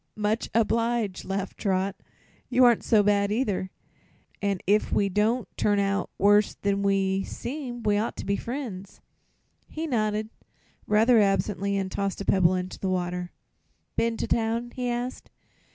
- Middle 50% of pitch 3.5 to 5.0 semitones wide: No, average, 2.8 semitones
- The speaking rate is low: No, average, 155 wpm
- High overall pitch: Yes, high, 205 Hz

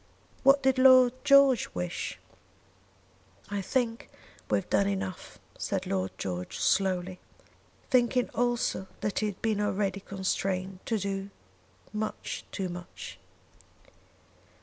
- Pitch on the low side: No, high, 200 Hz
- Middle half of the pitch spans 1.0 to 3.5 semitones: No, average, 4.4 semitones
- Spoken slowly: Yes, slow, 115 wpm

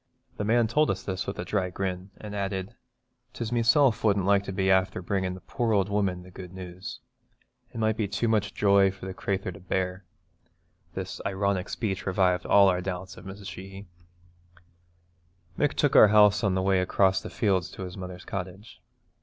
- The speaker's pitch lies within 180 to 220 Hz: No, very low, 95 Hz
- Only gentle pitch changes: Yes, narrow, 1.8 semitones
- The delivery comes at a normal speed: Yes, average, 190 wpm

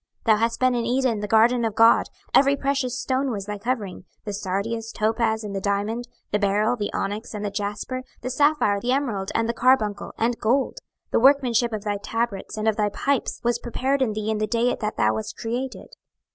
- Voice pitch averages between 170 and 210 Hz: No, high, 225 Hz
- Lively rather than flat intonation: No, average, 3.2 semitones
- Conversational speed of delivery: No, fast, 215 wpm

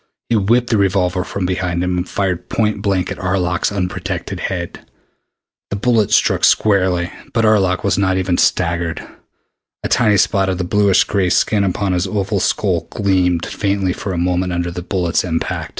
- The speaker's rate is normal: Yes, average, 170 wpm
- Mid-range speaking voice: No, very low, 95 Hz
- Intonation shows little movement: Yes, narrow, 2.1 semitones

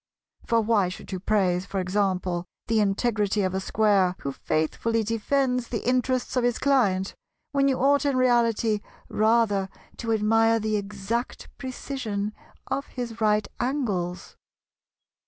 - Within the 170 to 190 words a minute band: No, slow, 135 wpm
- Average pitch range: Yes, average, 3.6 semitones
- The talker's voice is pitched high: Yes, high, 220 Hz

